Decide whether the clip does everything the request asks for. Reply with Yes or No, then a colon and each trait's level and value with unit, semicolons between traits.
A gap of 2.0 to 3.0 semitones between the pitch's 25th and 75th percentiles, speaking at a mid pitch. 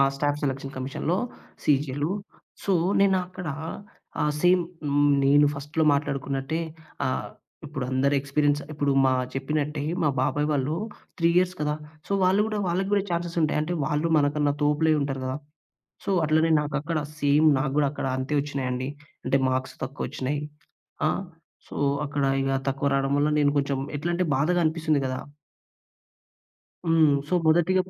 Yes: average, 2.7 semitones; medium, 145 Hz